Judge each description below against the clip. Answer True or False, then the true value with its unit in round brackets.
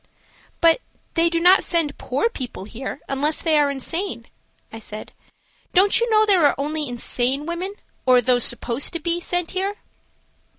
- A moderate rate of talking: True (170 wpm)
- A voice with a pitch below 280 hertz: False (310 Hz)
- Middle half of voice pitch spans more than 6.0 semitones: False (5.6 semitones)